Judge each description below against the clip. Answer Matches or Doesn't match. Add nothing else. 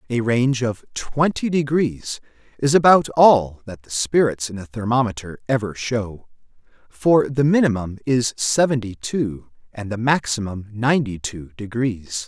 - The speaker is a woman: Doesn't match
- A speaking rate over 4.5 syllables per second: Doesn't match